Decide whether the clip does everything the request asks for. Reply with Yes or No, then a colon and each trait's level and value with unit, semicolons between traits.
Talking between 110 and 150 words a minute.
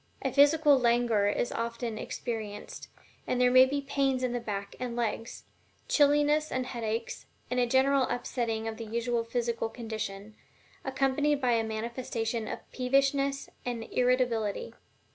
Yes: average, 145 wpm